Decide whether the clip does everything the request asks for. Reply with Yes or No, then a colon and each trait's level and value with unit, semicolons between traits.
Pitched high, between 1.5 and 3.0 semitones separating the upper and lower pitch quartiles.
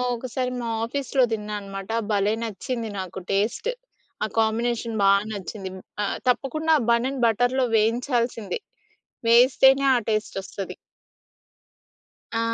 No: high, 230 Hz; average, 3.4 semitones